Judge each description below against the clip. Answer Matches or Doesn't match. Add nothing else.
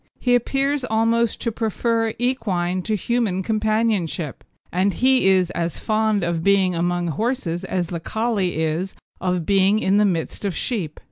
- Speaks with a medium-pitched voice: Doesn't match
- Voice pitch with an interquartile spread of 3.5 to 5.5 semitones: Matches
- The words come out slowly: Doesn't match